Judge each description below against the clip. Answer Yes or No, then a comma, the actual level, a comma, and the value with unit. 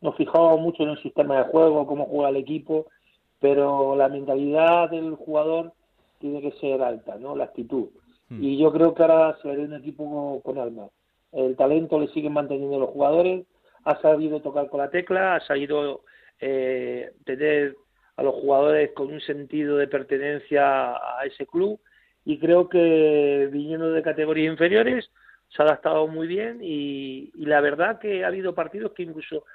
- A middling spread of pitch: No, narrow, 2.3 semitones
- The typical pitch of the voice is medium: Yes, medium, 150 Hz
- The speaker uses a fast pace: No, average, 175 wpm